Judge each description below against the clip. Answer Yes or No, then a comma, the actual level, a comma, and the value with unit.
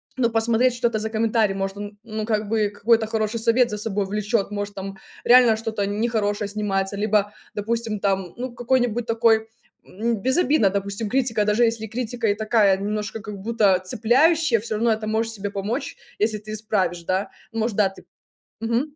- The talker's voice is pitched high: Yes, high, 220 Hz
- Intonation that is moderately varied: No, narrow, 2.2 semitones